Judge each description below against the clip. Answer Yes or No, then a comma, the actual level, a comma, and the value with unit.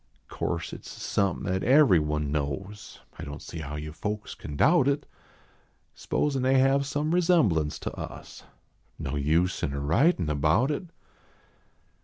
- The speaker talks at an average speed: Yes, average, 160 wpm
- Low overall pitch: Yes, very low, 95 Hz